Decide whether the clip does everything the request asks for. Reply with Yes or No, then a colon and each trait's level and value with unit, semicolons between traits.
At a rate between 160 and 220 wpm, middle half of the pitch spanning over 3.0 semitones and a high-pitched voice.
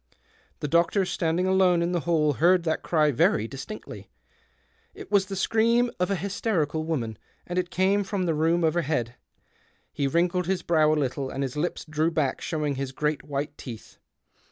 No: average, 180 wpm; average, 3.7 semitones; medium, 165 Hz